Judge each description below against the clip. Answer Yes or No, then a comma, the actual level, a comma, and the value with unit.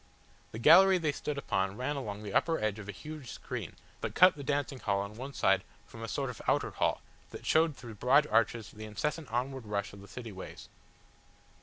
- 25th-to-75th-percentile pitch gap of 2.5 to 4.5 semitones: No, wide, 5.6 semitones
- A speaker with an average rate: No, fast, 210 wpm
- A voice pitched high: No, low, 120 Hz